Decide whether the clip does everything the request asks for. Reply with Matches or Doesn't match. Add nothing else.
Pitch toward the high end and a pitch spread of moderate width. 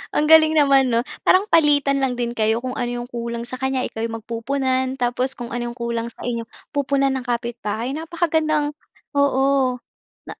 Matches